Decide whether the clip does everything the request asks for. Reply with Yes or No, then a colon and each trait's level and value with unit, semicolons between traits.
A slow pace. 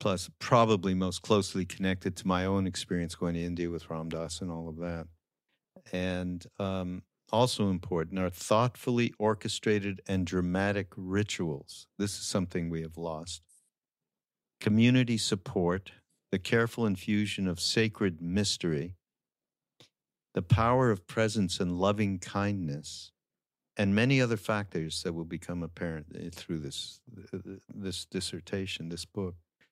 Yes: slow, 130 wpm